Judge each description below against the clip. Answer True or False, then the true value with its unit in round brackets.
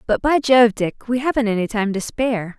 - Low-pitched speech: False (230 Hz)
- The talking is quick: True (230 wpm)